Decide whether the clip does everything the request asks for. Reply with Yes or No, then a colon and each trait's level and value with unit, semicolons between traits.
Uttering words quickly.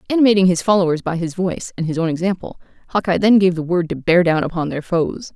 Yes: fast, 235 wpm